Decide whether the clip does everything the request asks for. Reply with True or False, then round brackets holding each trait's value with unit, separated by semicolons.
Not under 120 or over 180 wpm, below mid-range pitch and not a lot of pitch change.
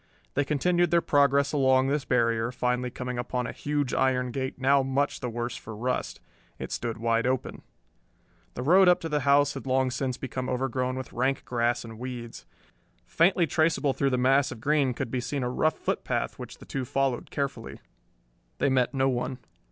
False (190 wpm; 130 Hz; 2.2 semitones)